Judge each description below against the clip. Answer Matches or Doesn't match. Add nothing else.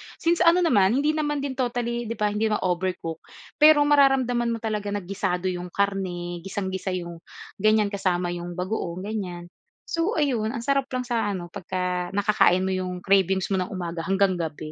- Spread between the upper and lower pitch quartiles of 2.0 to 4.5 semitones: Doesn't match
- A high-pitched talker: Matches